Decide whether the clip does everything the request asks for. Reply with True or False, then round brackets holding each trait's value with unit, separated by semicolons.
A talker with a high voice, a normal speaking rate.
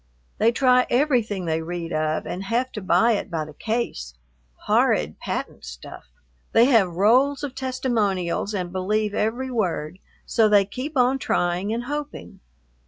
True (210 Hz; 155 wpm)